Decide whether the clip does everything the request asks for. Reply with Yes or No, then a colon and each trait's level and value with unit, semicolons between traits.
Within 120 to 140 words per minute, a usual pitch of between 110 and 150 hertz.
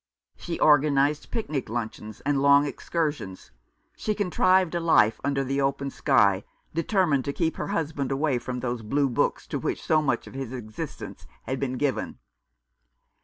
No: average, 160 wpm; medium, 140 Hz